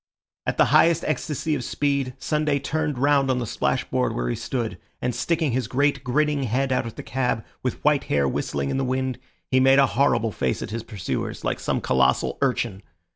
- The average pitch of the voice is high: No, low, 130 Hz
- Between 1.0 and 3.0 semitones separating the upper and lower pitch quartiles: No, average, 3.5 semitones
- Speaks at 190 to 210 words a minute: Yes, average, 200 wpm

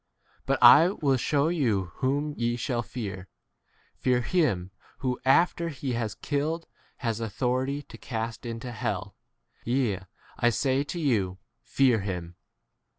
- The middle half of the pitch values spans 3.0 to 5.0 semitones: Yes, average, 4.2 semitones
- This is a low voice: Yes, low, 125 Hz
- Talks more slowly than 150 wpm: Yes, average, 140 wpm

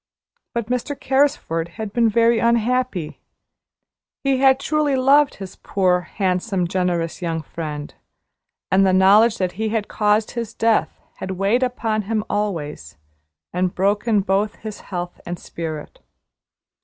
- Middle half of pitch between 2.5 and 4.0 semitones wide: No, average, 4.6 semitones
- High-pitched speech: Yes, high, 205 Hz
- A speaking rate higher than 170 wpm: No, slow, 135 wpm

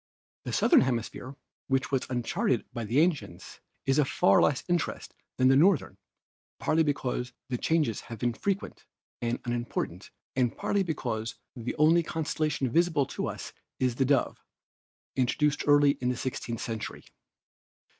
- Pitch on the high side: No, low, 130 Hz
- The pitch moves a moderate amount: Yes, average, 4.0 semitones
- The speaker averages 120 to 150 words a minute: Yes, average, 145 wpm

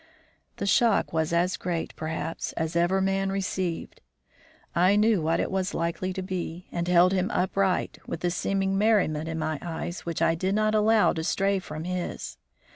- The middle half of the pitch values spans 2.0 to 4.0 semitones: Yes, narrow, 2.6 semitones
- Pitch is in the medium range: Yes, medium, 180 Hz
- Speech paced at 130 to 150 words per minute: No, average, 180 wpm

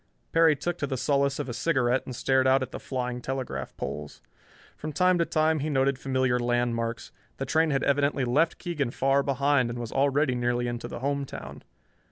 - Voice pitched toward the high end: No, low, 135 Hz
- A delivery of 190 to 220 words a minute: Yes, average, 200 wpm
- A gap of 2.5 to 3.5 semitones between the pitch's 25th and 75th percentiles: Yes, average, 2.8 semitones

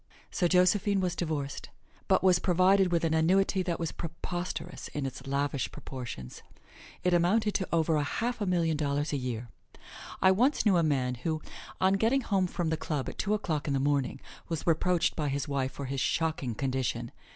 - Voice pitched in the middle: Yes, medium, 165 Hz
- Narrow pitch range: No, average, 4.6 semitones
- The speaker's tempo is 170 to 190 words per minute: Yes, average, 185 wpm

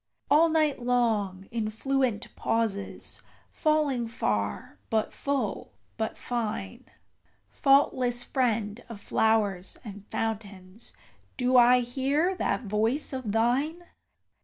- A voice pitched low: No, high, 235 Hz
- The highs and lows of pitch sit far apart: No, average, 4.0 semitones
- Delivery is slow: Yes, slow, 105 wpm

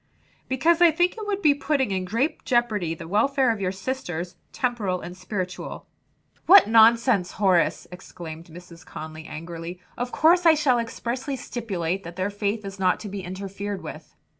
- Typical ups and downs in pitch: No, wide, 6.3 semitones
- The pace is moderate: Yes, average, 165 wpm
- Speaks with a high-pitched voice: Yes, high, 205 Hz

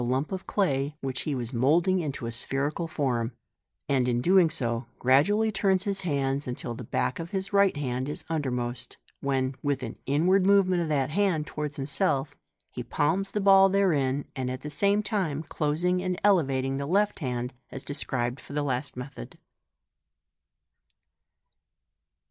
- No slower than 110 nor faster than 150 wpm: No, average, 160 wpm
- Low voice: No, medium, 145 Hz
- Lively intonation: Yes, wide, 5.9 semitones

